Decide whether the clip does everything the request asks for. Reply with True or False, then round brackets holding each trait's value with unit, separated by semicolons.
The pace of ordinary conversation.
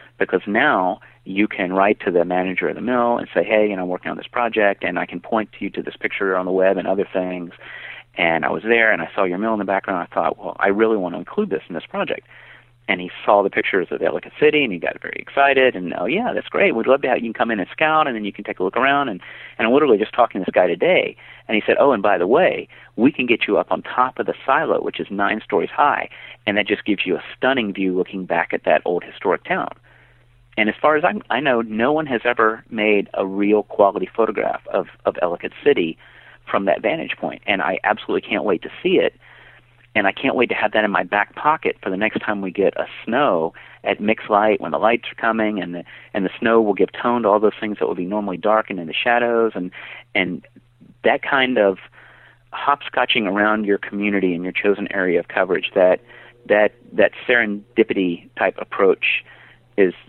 False (245 wpm)